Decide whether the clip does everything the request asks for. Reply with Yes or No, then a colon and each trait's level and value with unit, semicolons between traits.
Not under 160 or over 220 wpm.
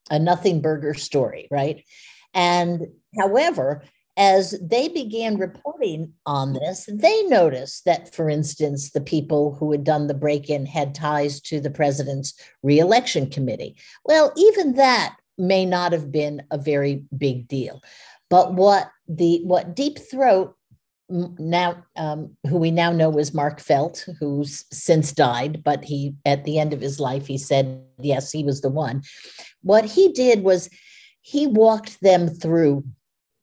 No: average, 150 wpm